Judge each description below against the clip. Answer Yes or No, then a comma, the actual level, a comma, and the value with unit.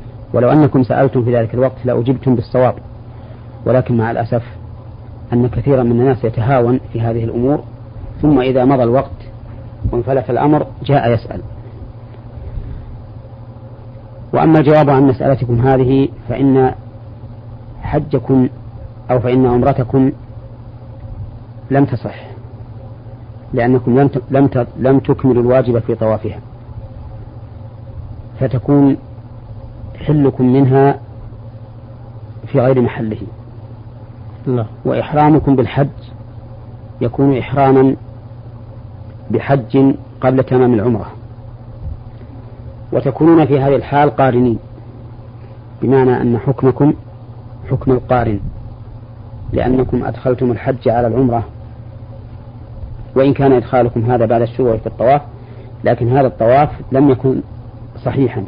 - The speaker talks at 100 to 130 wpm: No, average, 90 wpm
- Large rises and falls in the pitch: No, narrow, 2.5 semitones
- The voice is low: Yes, low, 120 Hz